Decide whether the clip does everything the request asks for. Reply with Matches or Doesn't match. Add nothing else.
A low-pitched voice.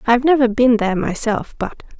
Doesn't match